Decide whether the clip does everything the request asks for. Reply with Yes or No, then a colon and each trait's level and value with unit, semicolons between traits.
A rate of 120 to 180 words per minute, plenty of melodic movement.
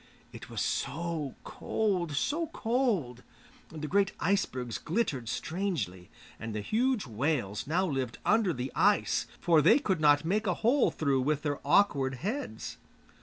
Yes: average, 145 wpm; wide, 7.2 semitones